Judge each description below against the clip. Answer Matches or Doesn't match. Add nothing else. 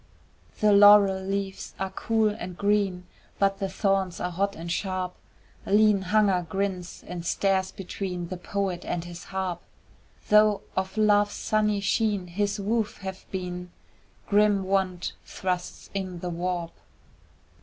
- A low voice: Doesn't match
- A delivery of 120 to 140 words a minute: Matches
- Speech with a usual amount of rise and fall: Doesn't match